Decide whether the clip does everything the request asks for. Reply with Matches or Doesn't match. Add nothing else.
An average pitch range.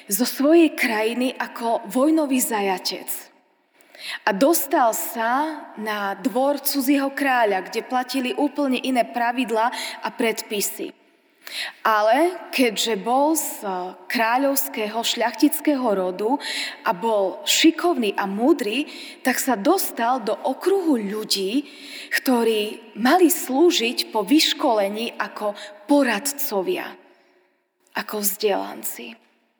Doesn't match